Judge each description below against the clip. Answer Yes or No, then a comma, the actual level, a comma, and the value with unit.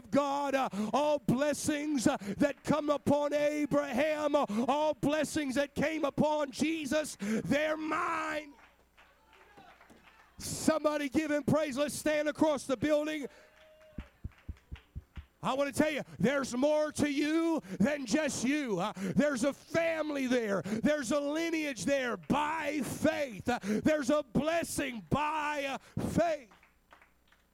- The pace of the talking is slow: Yes, slow, 120 wpm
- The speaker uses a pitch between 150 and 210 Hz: No, very high, 290 Hz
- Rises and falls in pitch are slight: Yes, narrow, 2.0 semitones